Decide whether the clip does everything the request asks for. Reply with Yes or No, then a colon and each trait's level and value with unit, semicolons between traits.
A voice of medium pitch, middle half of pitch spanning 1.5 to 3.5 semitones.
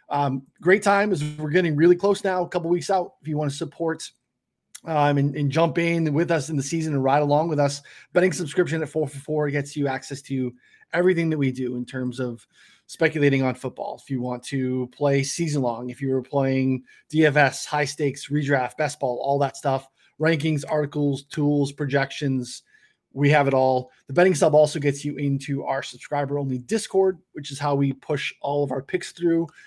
Yes: medium, 145 Hz; average, 3.1 semitones